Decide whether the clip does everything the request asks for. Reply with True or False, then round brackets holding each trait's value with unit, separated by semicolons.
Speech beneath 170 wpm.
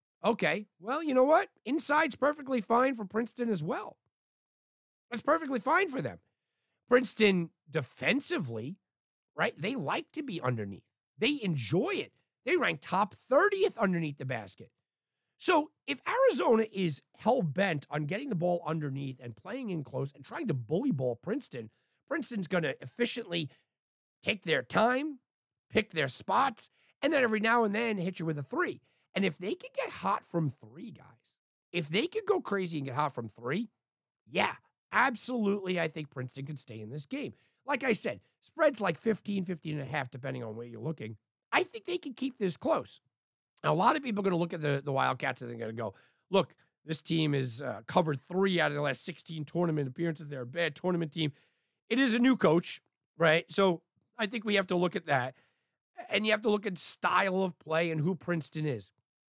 False (195 wpm)